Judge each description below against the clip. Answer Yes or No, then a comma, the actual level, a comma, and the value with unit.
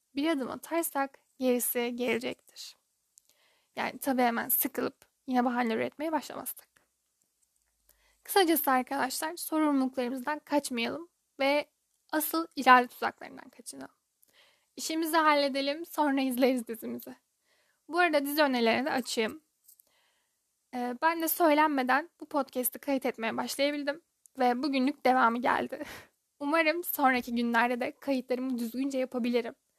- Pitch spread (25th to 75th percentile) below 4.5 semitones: Yes, average, 3.4 semitones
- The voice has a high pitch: Yes, very high, 275 Hz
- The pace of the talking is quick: No, average, 105 wpm